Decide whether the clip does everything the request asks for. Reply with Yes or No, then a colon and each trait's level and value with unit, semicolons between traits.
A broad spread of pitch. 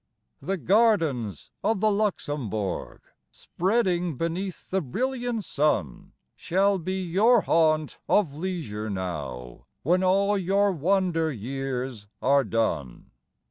Yes: wide, 7.8 semitones